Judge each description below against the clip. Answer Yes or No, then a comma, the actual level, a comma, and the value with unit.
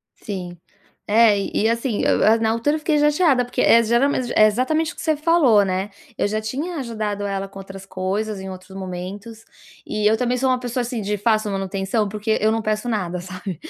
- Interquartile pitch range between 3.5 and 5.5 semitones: Yes, average, 3.9 semitones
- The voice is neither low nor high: No, high, 215 Hz